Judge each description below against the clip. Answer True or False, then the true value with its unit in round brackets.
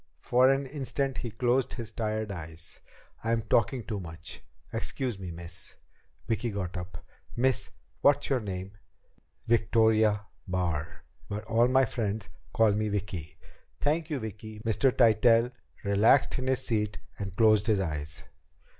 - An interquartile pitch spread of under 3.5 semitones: False (3.8 semitones)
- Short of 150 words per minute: True (140 wpm)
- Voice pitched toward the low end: True (110 Hz)